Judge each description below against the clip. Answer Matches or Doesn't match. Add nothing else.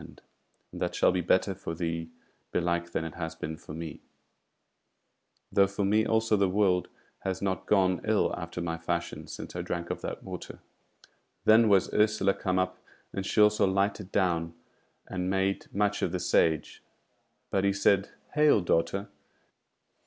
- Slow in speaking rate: Doesn't match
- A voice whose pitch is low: Matches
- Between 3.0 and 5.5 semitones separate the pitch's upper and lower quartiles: Doesn't match